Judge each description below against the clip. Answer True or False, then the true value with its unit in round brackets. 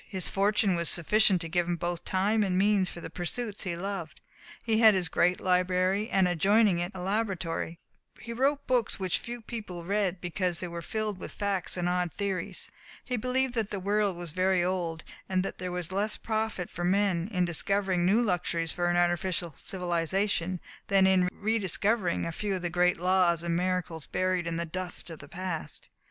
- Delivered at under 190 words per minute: False (195 wpm)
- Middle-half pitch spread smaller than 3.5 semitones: True (2.6 semitones)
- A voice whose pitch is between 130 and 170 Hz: False (185 Hz)